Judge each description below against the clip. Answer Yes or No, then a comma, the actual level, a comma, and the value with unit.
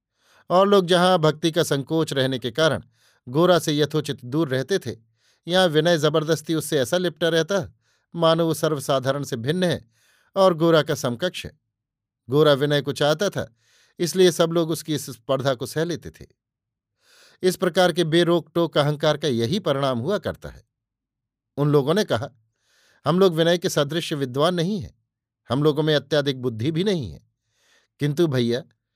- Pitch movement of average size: Yes, average, 4.9 semitones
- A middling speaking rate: Yes, average, 170 wpm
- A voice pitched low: No, medium, 150 Hz